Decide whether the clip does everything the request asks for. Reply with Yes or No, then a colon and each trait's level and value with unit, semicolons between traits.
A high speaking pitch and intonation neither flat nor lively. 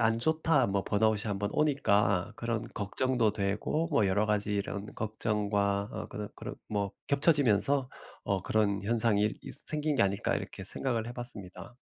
No: low, 110 Hz; average, 3.2 semitones